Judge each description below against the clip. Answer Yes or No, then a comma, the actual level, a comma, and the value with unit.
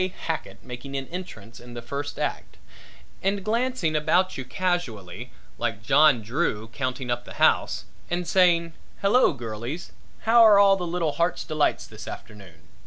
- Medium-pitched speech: Yes, medium, 155 Hz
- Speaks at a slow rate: No, average, 150 wpm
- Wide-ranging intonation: Yes, wide, 7.1 semitones